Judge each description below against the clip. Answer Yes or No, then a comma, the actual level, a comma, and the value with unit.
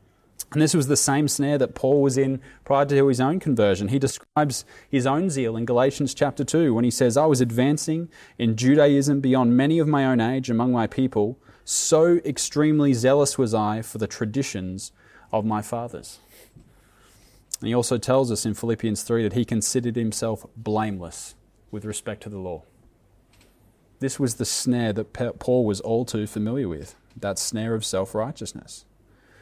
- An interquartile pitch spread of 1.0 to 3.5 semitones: No, average, 4.0 semitones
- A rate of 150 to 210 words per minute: Yes, average, 175 wpm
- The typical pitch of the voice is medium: No, low, 120 Hz